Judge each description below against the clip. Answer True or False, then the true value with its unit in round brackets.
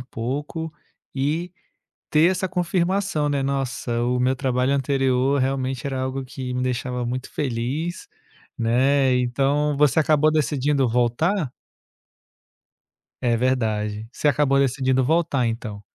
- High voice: False (135 Hz)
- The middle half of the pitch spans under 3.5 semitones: True (2.9 semitones)